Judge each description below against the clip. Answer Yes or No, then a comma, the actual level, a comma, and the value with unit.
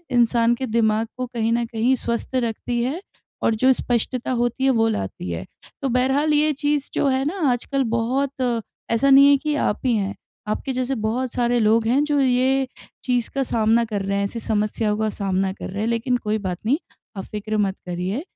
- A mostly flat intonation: No, average, 3.4 semitones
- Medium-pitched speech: No, high, 235 Hz